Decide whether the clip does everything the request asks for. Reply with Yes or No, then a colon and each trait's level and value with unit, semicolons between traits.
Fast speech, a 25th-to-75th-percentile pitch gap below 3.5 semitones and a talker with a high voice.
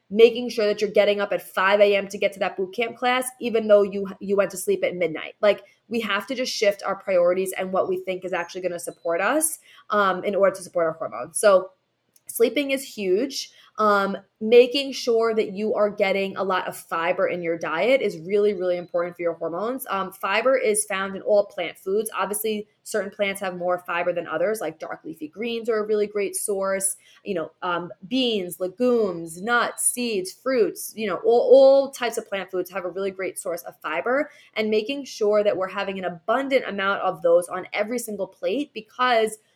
No: fast, 210 wpm; average, 3.8 semitones; high, 205 Hz